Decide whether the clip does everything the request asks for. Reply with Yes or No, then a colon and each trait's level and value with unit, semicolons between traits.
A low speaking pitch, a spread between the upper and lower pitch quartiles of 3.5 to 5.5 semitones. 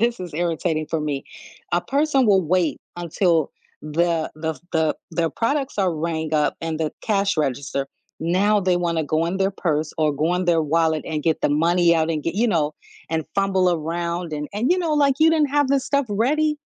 No: medium, 170 Hz; average, 4.3 semitones